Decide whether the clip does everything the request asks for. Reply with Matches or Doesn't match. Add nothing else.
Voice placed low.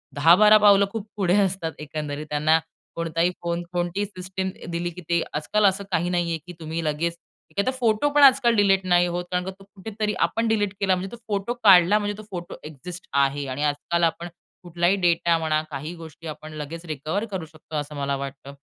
Doesn't match